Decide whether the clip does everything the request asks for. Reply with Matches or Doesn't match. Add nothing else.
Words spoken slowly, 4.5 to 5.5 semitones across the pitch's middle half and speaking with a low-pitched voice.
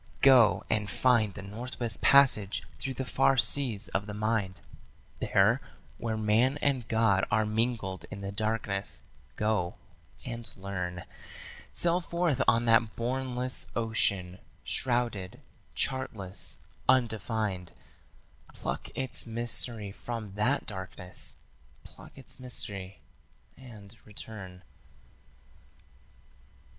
Doesn't match